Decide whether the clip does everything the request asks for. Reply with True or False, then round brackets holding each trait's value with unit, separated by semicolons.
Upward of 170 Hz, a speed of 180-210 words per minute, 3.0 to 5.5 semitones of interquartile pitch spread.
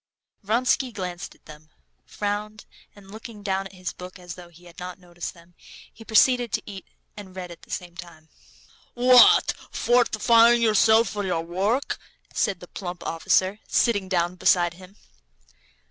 False (190 Hz; 160 wpm; 3.7 semitones)